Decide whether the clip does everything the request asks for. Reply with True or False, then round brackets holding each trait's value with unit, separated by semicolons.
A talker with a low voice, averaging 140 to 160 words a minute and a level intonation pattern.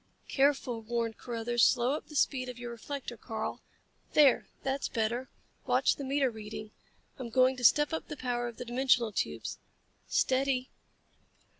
False (250 Hz; 155 wpm; 2.3 semitones)